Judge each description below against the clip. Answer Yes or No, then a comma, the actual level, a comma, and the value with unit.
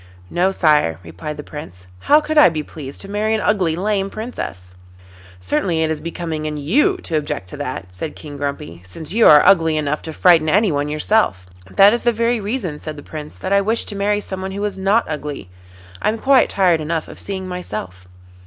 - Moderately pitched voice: Yes, medium, 165 Hz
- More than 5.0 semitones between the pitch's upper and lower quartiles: Yes, wide, 5.4 semitones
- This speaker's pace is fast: Yes, fast, 210 wpm